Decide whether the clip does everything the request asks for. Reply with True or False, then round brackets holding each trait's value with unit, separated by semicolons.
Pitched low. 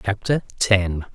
True (100 Hz)